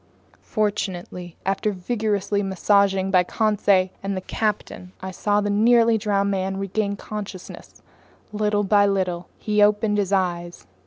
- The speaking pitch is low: No, high, 200 Hz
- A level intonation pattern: Yes, narrow, 1.8 semitones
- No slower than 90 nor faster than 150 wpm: Yes, slow, 135 wpm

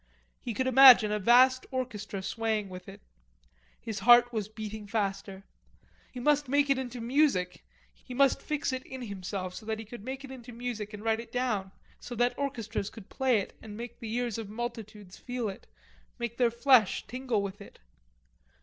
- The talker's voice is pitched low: No, high, 230 Hz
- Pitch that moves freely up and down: No, average, 3.4 semitones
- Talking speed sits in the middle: Yes, average, 185 wpm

